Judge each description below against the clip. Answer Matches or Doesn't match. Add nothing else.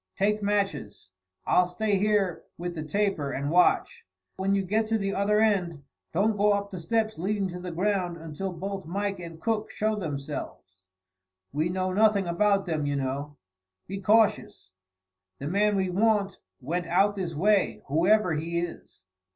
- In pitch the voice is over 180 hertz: Matches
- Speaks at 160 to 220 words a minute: Matches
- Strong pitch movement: Doesn't match